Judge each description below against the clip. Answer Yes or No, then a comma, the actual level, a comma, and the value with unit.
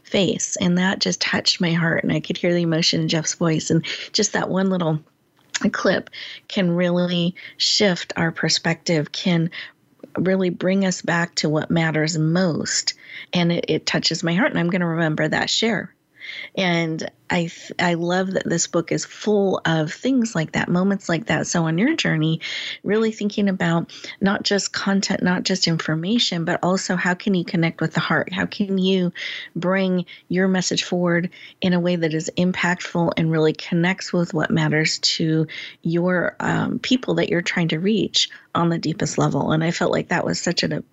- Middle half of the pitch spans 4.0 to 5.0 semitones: No, narrow, 2.6 semitones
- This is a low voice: No, medium, 175 Hz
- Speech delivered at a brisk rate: No, average, 185 wpm